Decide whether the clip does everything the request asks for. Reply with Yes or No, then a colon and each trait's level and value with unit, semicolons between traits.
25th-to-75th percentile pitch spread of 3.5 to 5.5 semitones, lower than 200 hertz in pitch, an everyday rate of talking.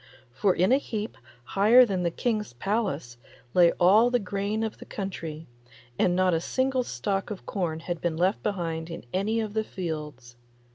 Yes: average, 4.4 semitones; high, 190 Hz; average, 180 wpm